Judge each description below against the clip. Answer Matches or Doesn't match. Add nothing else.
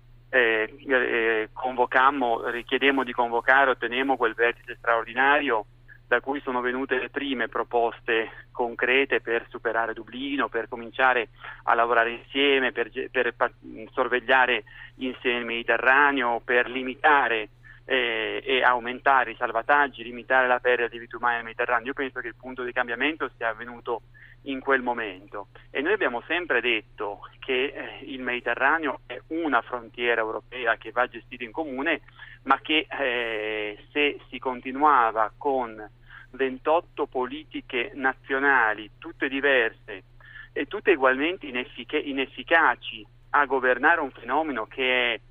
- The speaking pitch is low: Matches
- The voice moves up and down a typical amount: Doesn't match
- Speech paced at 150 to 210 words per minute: Doesn't match